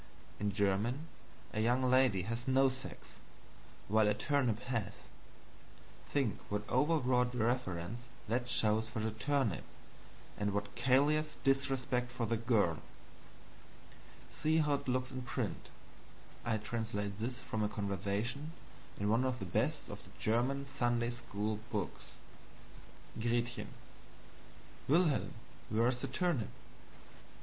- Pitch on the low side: Yes, low, 120 Hz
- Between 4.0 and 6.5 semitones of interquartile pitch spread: No, average, 3.5 semitones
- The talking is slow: Yes, slow, 125 wpm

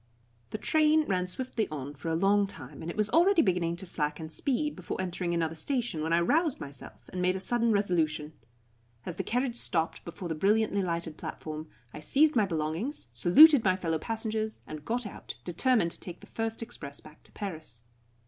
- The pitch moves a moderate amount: No, wide, 5.9 semitones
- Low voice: No, medium, 185 Hz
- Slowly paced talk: No, average, 195 wpm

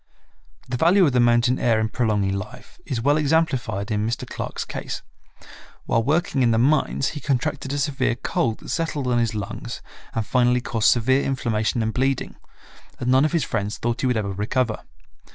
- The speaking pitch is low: Yes, low, 125 Hz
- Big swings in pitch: No, average, 3.4 semitones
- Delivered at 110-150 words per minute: No, average, 190 wpm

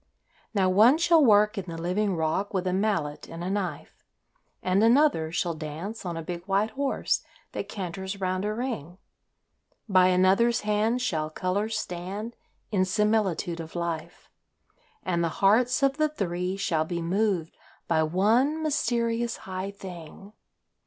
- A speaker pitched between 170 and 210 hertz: Yes, high, 190 Hz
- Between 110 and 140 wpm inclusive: No, average, 150 wpm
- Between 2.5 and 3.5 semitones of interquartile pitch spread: No, average, 4.1 semitones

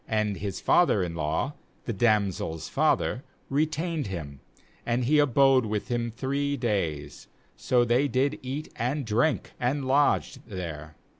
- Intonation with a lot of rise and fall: Yes, wide, 6.2 semitones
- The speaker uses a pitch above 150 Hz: No, low, 120 Hz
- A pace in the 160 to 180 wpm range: No, average, 140 wpm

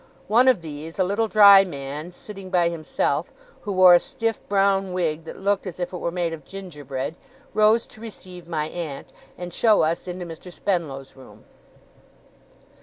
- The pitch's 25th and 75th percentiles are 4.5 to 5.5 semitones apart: No, average, 3.5 semitones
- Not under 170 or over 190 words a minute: Yes, average, 175 wpm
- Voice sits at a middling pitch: Yes, medium, 180 Hz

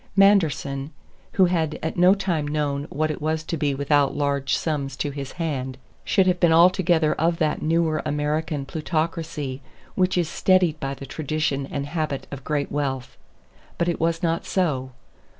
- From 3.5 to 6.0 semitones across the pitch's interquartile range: No, average, 2.9 semitones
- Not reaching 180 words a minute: Yes, average, 170 wpm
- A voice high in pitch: No, medium, 155 Hz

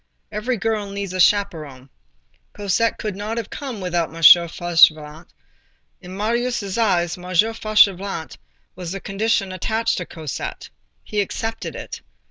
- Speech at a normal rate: No, slow, 130 wpm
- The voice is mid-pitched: No, high, 195 Hz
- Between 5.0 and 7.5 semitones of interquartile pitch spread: No, average, 4.0 semitones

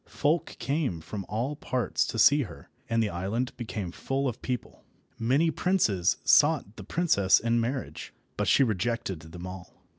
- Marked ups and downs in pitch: Yes, wide, 6.1 semitones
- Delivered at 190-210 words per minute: No, average, 160 wpm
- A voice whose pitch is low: Yes, low, 115 Hz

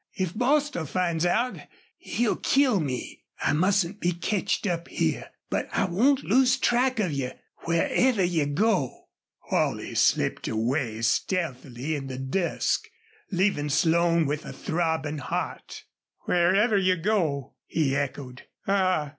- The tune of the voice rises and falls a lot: Yes, wide, 5.7 semitones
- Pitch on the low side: No, medium, 170 Hz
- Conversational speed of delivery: No, slow, 130 wpm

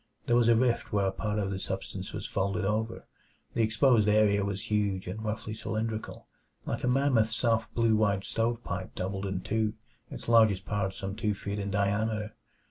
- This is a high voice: No, low, 105 Hz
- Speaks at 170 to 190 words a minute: Yes, average, 185 wpm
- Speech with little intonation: Yes, narrow, 2.1 semitones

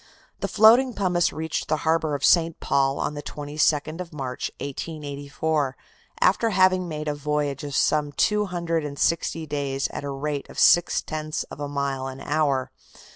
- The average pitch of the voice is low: No, medium, 150 Hz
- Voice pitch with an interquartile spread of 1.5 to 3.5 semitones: Yes, narrow, 2.6 semitones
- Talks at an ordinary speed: Yes, average, 175 wpm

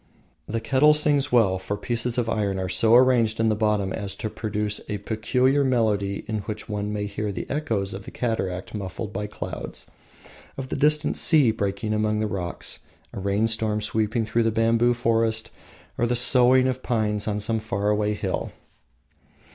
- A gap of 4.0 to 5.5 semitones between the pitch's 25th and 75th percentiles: No, narrow, 2.5 semitones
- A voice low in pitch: Yes, low, 110 Hz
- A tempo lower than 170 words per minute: No, average, 180 wpm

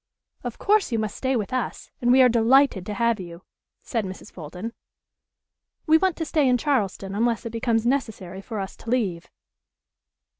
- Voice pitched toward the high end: Yes, high, 230 Hz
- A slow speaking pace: No, average, 180 wpm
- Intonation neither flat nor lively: Yes, average, 4.6 semitones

